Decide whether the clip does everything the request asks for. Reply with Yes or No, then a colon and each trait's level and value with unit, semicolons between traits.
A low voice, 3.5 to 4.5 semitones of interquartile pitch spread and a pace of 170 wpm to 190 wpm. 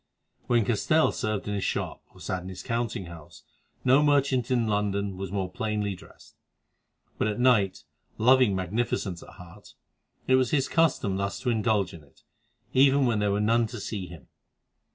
Yes: low, 105 Hz; average, 4.2 semitones; average, 175 wpm